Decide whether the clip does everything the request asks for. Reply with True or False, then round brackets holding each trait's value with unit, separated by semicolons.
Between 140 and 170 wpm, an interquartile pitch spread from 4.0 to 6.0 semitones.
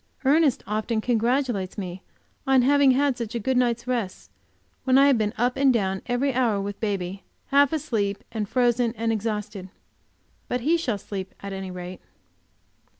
True (160 wpm; 4.4 semitones)